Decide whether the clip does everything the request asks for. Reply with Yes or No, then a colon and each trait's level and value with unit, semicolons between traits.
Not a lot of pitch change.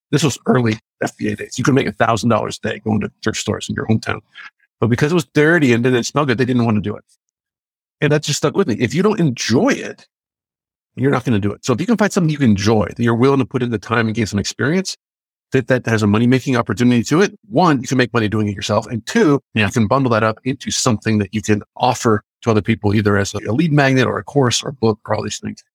No: average, 4.2 semitones